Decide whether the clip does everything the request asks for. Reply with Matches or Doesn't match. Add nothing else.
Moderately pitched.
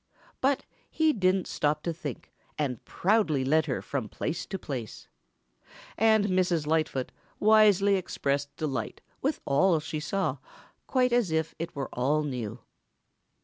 Matches